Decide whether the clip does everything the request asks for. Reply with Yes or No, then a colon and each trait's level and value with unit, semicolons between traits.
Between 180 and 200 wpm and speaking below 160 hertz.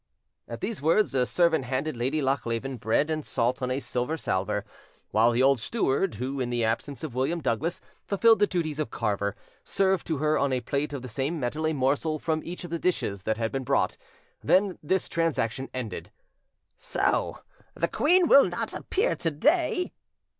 Yes: average, 190 wpm; medium, 140 Hz